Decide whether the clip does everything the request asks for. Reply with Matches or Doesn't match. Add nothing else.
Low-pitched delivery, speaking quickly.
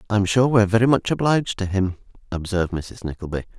Matches